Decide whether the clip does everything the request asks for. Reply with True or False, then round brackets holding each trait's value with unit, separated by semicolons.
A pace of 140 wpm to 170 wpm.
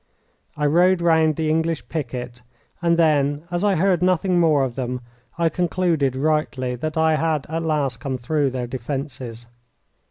True (160 wpm)